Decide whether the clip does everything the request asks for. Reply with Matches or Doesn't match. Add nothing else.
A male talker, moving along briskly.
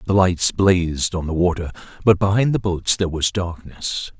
Doesn't match